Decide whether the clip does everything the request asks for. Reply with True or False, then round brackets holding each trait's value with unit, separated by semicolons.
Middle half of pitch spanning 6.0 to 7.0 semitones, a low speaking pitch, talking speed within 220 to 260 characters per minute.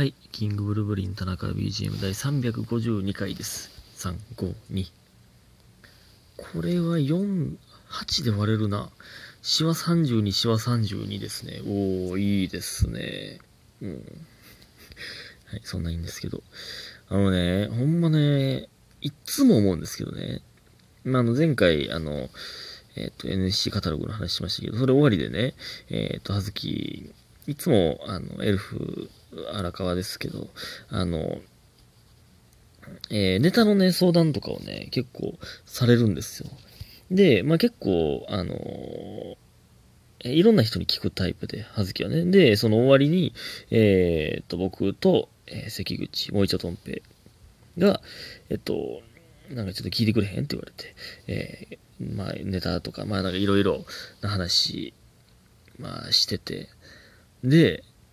True (6.3 semitones; 105 Hz; 255 characters per minute)